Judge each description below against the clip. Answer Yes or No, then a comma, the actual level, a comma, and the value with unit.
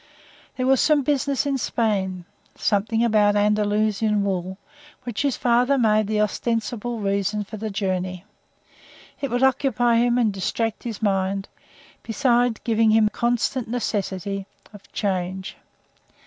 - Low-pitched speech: No, high, 215 Hz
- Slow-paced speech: Yes, slow, 130 wpm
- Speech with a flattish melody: No, average, 3.3 semitones